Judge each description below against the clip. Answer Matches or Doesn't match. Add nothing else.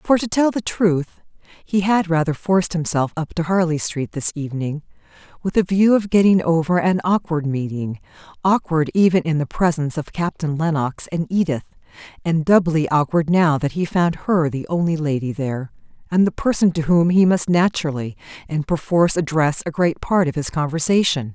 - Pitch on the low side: Doesn't match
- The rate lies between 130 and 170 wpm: Doesn't match